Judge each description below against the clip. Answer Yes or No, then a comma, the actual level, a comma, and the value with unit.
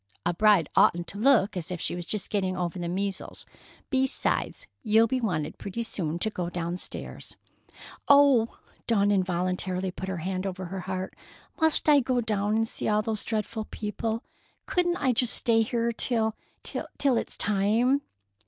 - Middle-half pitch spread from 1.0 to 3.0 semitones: No, average, 4.0 semitones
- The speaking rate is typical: Yes, average, 160 wpm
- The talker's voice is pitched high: Yes, high, 210 Hz